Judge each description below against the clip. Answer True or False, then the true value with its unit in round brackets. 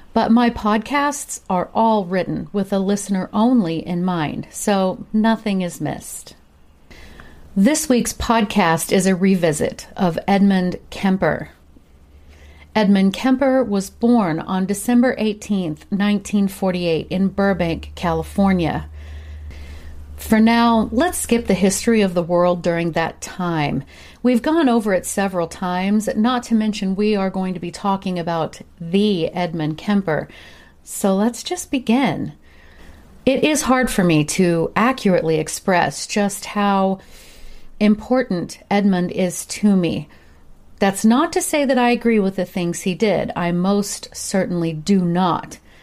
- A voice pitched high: True (195 Hz)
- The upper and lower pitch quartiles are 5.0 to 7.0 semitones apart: False (4.5 semitones)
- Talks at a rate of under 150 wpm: True (135 wpm)